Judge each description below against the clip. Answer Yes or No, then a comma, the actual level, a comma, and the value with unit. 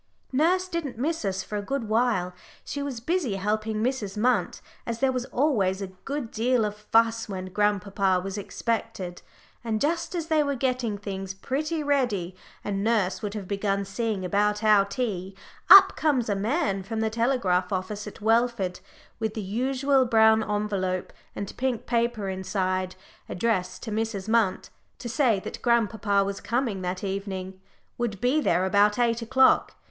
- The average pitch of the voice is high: Yes, high, 215 Hz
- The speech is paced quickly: No, average, 165 wpm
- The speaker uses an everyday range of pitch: Yes, average, 4.0 semitones